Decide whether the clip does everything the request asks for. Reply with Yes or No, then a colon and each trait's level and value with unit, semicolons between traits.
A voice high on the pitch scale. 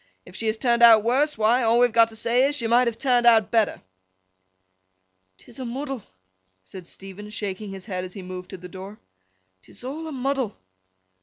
Yes: high, 230 Hz